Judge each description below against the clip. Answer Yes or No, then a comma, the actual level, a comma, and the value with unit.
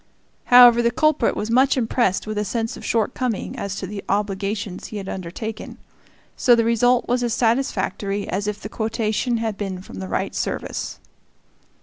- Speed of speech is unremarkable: Yes, average, 175 wpm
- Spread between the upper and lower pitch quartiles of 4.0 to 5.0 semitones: No, average, 3.1 semitones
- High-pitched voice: Yes, high, 220 Hz